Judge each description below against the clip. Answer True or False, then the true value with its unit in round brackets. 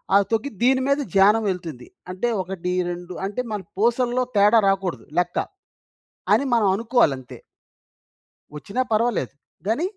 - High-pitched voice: True (205 Hz)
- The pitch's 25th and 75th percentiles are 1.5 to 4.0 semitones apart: False (4.9 semitones)